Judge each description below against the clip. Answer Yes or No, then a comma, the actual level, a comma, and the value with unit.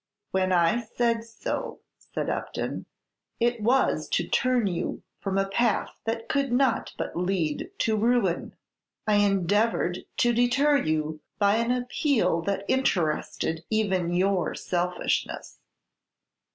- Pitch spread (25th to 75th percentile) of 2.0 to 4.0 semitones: No, average, 5.0 semitones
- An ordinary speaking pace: No, slow, 125 wpm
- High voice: Yes, high, 210 Hz